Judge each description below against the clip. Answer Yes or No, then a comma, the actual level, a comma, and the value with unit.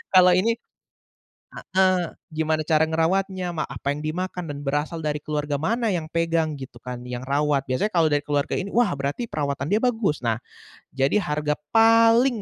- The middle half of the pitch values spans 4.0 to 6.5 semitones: Yes, average, 4.6 semitones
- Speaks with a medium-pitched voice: Yes, medium, 155 Hz